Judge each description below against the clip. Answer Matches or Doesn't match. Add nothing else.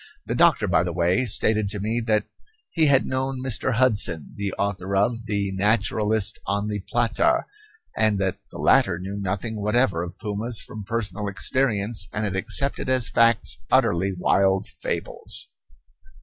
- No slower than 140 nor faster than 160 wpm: Matches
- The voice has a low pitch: Matches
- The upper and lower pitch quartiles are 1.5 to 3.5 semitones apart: Matches